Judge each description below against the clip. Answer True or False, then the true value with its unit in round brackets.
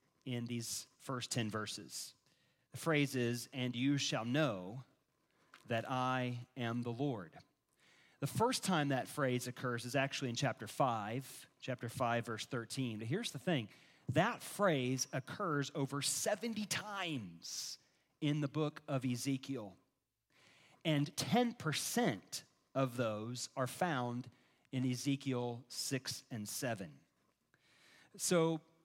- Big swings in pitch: False (3.5 semitones)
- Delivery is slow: True (125 wpm)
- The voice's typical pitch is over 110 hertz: True (135 Hz)